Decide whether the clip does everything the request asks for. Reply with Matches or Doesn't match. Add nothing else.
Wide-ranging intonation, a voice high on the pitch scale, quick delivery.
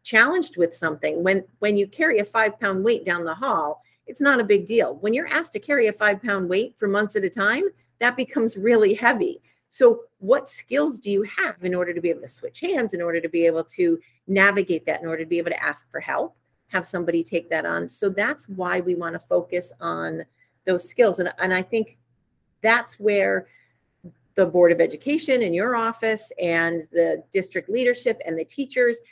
Matches